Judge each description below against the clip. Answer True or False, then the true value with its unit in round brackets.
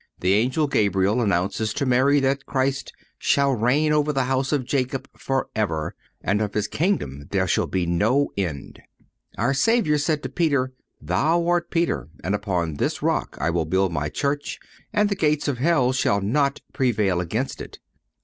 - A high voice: False (130 Hz)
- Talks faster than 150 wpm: True (170 wpm)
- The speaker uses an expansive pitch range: True (6.5 semitones)